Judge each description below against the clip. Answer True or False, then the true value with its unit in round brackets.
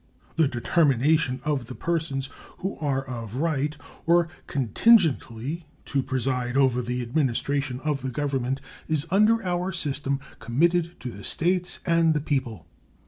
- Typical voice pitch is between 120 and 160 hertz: True (140 Hz)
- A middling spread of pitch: True (4.5 semitones)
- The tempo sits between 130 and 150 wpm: True (140 wpm)